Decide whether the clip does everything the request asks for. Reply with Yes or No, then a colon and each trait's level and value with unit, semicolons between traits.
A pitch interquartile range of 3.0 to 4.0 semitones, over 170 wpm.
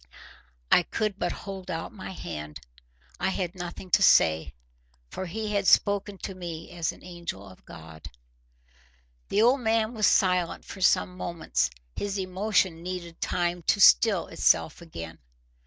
No: average, 3.3 semitones; average, 150 wpm